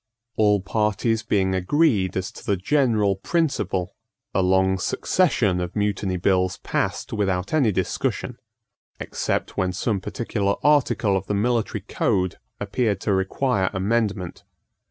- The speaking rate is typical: No, slow, 130 wpm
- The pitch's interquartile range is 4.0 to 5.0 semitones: No, average, 3.1 semitones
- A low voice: Yes, low, 100 Hz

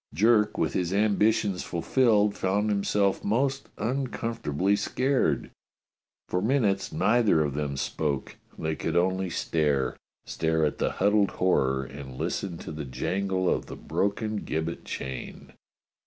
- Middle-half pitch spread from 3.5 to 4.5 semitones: No, average, 5.2 semitones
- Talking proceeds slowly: Yes, slow, 130 wpm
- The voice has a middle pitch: No, very low, 95 Hz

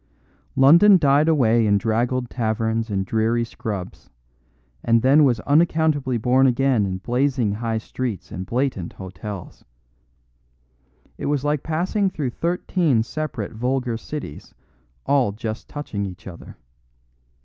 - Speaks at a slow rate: Yes, slow, 125 wpm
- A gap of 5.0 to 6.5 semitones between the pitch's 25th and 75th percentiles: No, average, 4.6 semitones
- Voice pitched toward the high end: No, low, 120 Hz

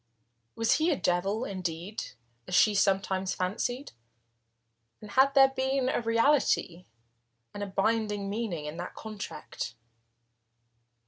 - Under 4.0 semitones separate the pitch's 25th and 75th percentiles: No, average, 4.3 semitones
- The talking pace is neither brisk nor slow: No, slow, 120 wpm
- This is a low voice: No, high, 205 Hz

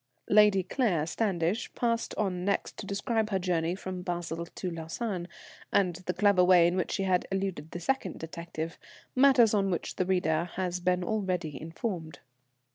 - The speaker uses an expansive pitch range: No, average, 2.9 semitones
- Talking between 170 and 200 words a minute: No, average, 160 wpm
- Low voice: No, medium, 185 Hz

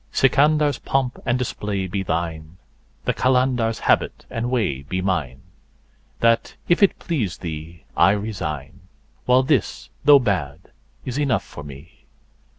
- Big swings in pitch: Yes, wide, 7.6 semitones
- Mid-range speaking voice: No, low, 105 Hz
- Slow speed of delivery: Yes, slow, 130 wpm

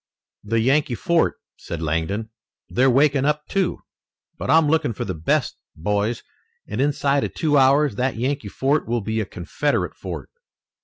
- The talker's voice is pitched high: No, low, 130 Hz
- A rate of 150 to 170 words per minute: Yes, average, 160 wpm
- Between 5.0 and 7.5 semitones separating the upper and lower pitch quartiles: Yes, wide, 5.6 semitones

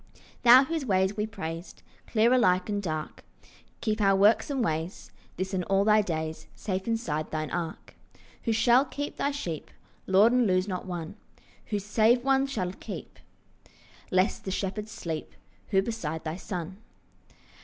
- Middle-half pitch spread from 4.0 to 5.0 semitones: Yes, average, 4.3 semitones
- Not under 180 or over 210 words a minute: No, average, 155 wpm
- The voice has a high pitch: Yes, high, 195 Hz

